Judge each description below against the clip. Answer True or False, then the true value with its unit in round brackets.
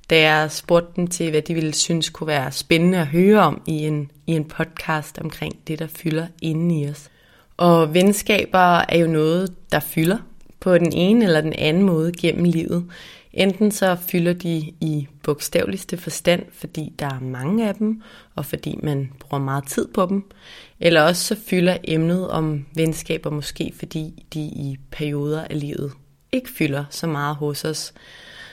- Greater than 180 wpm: False (175 wpm)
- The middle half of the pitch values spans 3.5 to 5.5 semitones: False (2.6 semitones)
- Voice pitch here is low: False (160 Hz)